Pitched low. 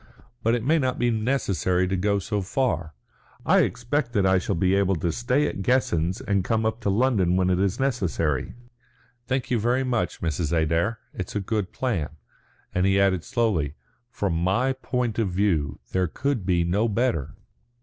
Yes: low, 100 Hz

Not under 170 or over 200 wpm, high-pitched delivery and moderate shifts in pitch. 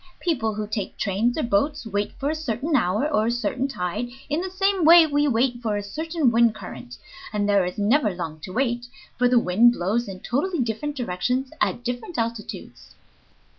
No: average, 195 wpm; high, 235 Hz; wide, 5.8 semitones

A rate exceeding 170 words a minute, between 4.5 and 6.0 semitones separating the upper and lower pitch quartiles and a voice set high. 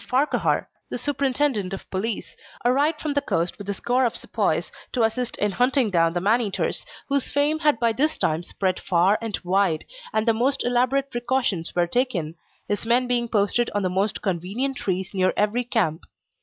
Yes: average, 185 wpm; average, 5.1 semitones; high, 225 Hz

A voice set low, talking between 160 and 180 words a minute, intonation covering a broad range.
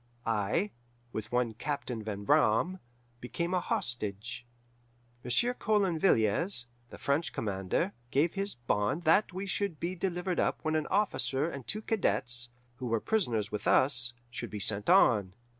No: low, 130 Hz; average, 150 wpm; wide, 8.2 semitones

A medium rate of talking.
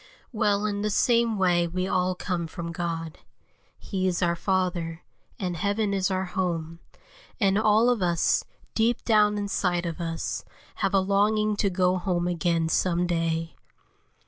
Yes: average, 155 wpm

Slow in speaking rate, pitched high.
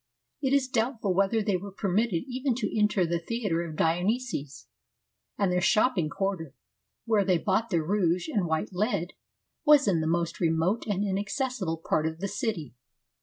No: average, 170 wpm; high, 195 Hz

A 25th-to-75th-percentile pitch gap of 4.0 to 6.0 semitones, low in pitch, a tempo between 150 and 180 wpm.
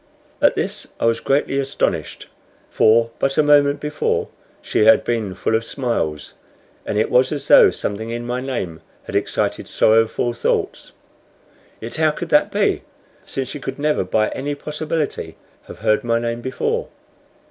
Yes: average, 4.3 semitones; low, 125 Hz; average, 160 wpm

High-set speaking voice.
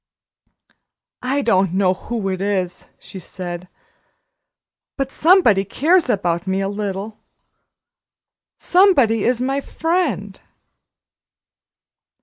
Yes: high, 205 Hz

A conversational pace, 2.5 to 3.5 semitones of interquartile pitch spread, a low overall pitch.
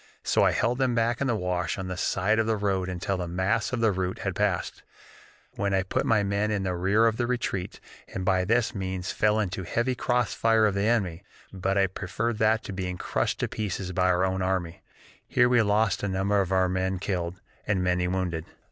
No: fast, 230 wpm; average, 3.0 semitones; very low, 95 Hz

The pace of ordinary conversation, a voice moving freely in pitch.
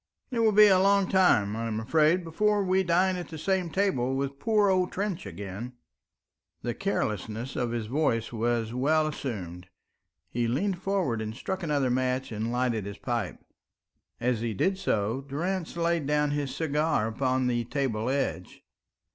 Yes: average, 165 wpm; wide, 7.7 semitones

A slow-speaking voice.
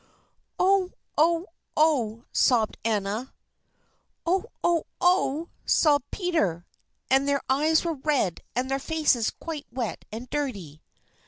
Yes: slow, 115 wpm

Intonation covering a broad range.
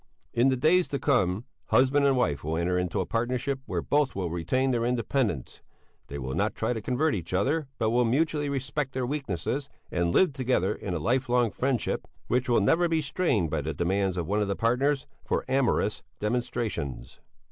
Yes: wide, 6.6 semitones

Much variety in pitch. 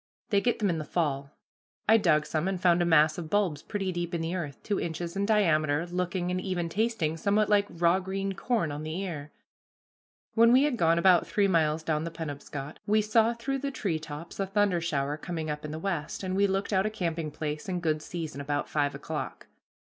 No: average, 4.3 semitones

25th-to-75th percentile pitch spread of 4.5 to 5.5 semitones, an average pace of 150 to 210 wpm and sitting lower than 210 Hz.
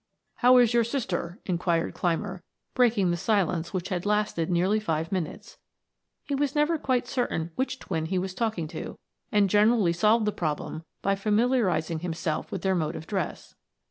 Yes: average, 4.9 semitones; average, 170 wpm; high, 190 Hz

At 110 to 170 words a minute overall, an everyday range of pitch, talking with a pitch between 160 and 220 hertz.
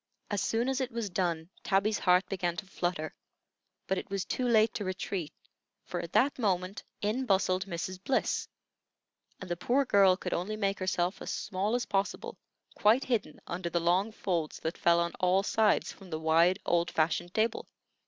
No: average, 185 wpm; average, 3.5 semitones; high, 190 Hz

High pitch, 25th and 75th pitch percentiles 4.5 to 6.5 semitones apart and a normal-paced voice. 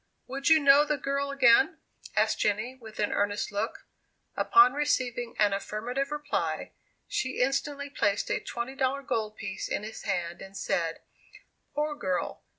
Yes: very high, 250 Hz; average, 5.0 semitones; average, 150 wpm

